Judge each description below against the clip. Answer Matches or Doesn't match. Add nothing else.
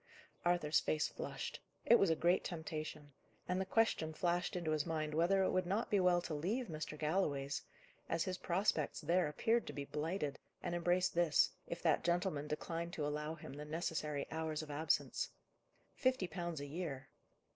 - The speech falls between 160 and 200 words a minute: Matches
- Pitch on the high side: Doesn't match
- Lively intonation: Doesn't match